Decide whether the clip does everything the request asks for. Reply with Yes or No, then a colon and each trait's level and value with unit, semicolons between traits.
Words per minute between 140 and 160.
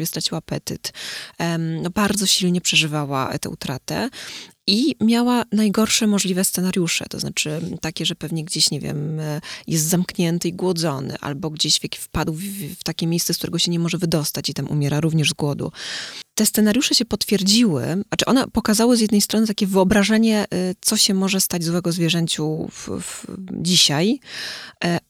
Yes: average, 155 wpm